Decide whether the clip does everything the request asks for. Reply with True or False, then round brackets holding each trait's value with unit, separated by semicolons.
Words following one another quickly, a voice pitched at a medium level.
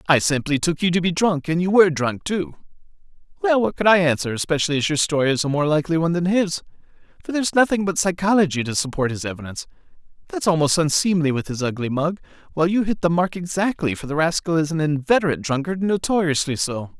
True (210 wpm; 165 Hz)